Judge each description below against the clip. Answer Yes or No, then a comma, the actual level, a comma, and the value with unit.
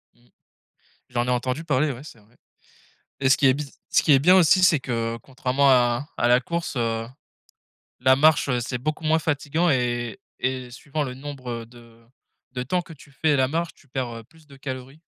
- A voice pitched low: Yes, low, 130 Hz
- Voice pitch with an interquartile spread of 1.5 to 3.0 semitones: No, average, 3.6 semitones